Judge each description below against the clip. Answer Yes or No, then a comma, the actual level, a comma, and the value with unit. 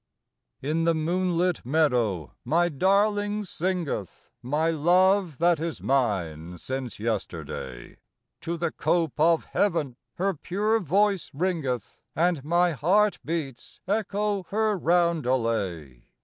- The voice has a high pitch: No, medium, 165 Hz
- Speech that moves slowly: Yes, slow, 115 wpm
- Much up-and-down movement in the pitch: Yes, wide, 6.1 semitones